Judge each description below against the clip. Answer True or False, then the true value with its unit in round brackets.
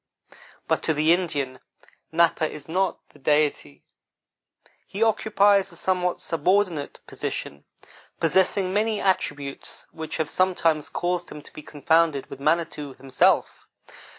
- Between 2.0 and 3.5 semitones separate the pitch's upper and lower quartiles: False (4.0 semitones)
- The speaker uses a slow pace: True (125 wpm)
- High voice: False (165 Hz)